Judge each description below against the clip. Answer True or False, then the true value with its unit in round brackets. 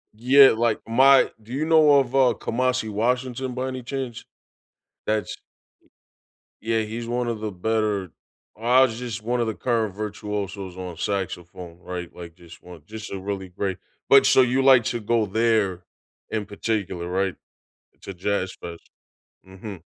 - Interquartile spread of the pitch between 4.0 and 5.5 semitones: True (4.3 semitones)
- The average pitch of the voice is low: True (110 Hz)